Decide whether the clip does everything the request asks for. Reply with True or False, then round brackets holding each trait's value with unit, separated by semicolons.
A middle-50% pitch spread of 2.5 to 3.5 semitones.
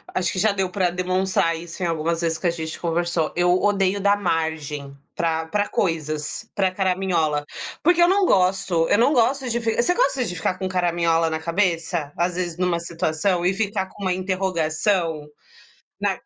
True (2.8 semitones)